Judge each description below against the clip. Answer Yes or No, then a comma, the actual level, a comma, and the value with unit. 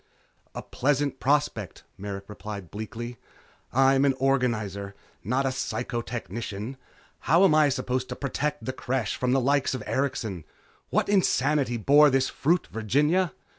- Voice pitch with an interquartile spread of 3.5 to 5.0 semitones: Yes, average, 4.0 semitones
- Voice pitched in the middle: No, low, 130 Hz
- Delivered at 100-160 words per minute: Yes, average, 140 wpm